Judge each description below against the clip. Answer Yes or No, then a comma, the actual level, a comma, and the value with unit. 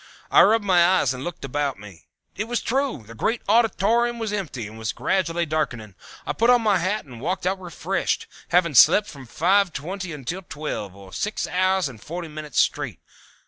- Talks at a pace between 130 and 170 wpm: No, average, 190 wpm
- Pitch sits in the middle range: Yes, medium, 175 Hz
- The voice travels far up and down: Yes, wide, 6.6 semitones